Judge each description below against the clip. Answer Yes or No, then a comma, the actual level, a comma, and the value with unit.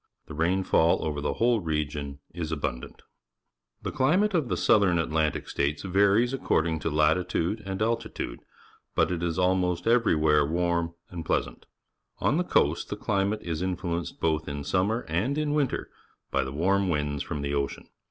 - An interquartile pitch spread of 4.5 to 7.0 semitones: Yes, average, 4.8 semitones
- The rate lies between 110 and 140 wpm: No, average, 160 wpm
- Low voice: Yes, very low, 85 Hz